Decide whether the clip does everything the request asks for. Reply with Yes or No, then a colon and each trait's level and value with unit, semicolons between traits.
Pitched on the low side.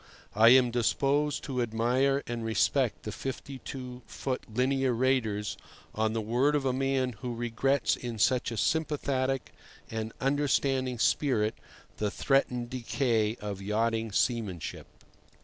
Yes: low, 125 Hz